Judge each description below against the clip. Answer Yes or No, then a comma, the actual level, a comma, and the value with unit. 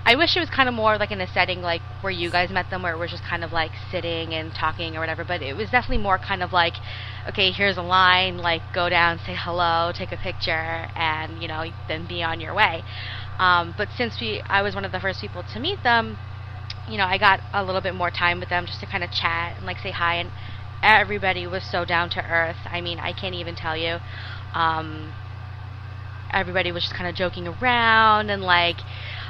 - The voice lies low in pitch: Yes, low, 105 Hz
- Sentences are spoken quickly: Yes, fast, 235 wpm